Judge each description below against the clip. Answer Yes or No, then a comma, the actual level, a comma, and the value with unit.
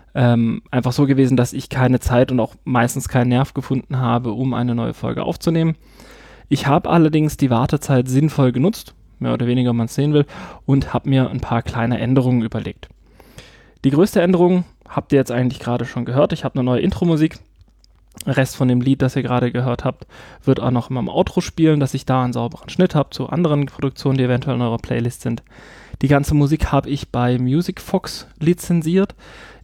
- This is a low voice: Yes, low, 130 Hz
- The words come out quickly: Yes, fast, 200 wpm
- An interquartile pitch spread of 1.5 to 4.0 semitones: Yes, average, 3.0 semitones